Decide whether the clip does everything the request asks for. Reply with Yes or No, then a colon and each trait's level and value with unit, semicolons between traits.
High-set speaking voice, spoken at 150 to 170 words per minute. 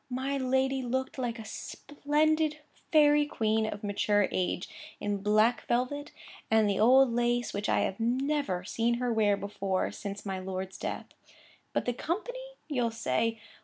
Yes: high, 235 Hz; average, 155 wpm